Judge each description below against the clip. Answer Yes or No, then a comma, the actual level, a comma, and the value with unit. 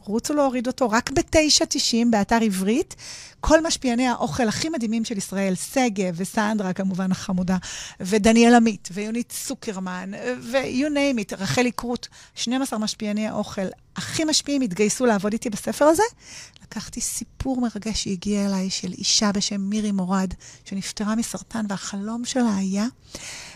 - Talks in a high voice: Yes, high, 220 Hz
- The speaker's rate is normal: Yes, average, 135 wpm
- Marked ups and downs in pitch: No, average, 3.8 semitones